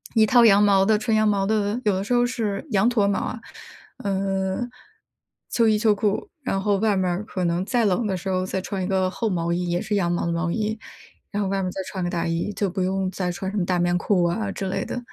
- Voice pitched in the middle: No, high, 195 Hz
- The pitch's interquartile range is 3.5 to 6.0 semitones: No, narrow, 2.5 semitones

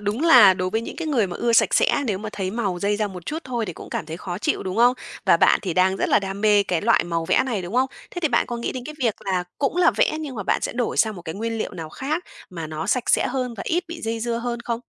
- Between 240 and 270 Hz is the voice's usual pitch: No, high, 220 Hz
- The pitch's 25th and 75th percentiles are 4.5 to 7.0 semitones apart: Yes, average, 4.8 semitones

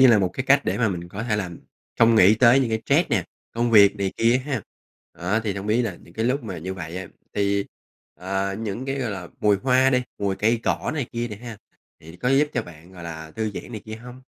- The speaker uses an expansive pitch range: No, average, 4.0 semitones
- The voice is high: No, low, 110 Hz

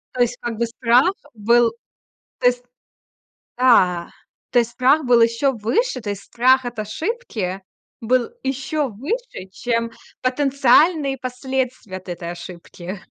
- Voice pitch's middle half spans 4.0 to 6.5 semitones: No, average, 3.6 semitones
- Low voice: No, high, 245 Hz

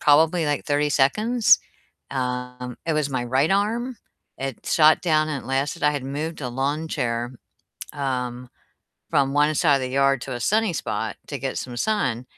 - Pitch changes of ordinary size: Yes, average, 3.6 semitones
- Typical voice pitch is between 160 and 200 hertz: No, medium, 140 Hz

